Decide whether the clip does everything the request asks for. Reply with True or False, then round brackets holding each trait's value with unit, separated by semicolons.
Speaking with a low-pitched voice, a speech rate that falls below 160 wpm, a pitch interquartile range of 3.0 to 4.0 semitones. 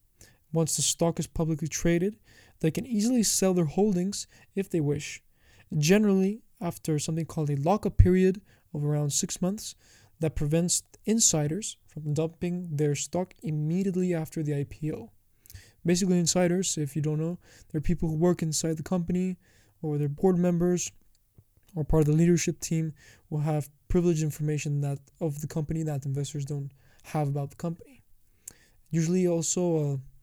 False (160 Hz; 150 wpm; 3.5 semitones)